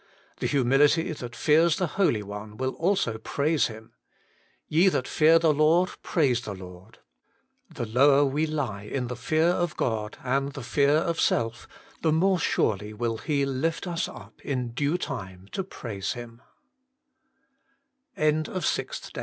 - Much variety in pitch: Yes, wide, 5.7 semitones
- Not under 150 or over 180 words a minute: No, average, 140 wpm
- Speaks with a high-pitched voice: No, medium, 140 Hz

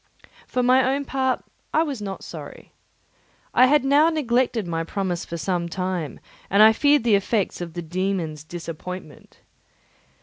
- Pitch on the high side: Yes, high, 200 Hz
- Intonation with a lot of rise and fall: Yes, wide, 6.9 semitones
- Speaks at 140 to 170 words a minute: Yes, average, 155 wpm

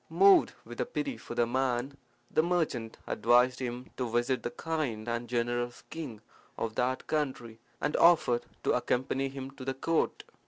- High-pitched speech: No, low, 130 Hz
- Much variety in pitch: No, average, 3.7 semitones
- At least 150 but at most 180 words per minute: Yes, average, 160 wpm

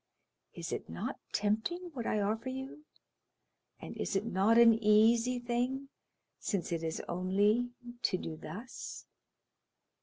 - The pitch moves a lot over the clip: No, average, 3.8 semitones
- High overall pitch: Yes, high, 225 Hz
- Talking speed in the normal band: No, slow, 130 wpm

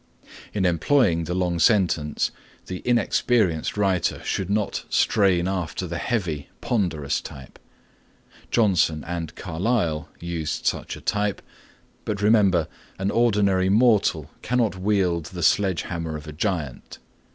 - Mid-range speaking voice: No, very low, 95 Hz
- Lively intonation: No, average, 3.7 semitones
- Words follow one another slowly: Yes, slow, 125 wpm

